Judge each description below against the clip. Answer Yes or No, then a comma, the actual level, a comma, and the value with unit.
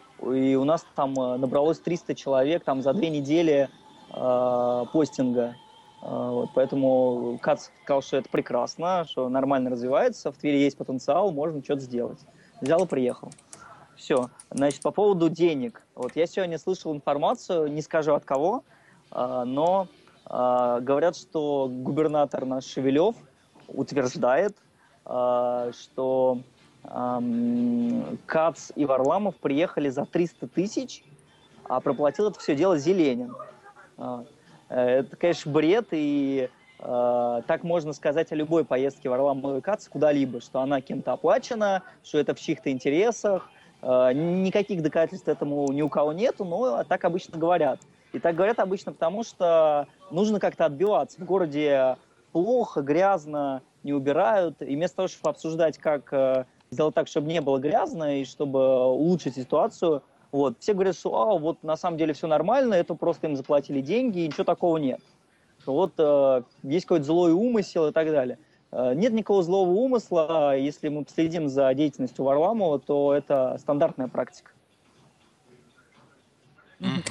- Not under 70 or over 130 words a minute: No, average, 140 wpm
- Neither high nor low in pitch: Yes, medium, 150 Hz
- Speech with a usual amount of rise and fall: Yes, average, 4.5 semitones